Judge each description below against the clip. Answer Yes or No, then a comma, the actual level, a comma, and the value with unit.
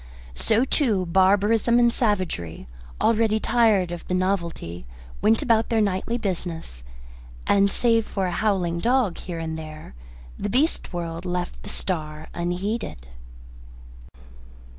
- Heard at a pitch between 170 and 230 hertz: Yes, high, 190 Hz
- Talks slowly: Yes, slow, 125 wpm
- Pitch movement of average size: Yes, average, 4.7 semitones